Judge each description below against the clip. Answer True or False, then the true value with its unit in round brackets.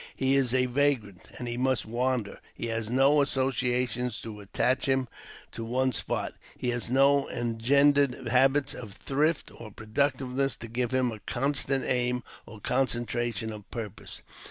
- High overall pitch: False (125 Hz)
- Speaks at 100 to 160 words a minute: True (155 wpm)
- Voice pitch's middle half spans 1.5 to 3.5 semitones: True (2.5 semitones)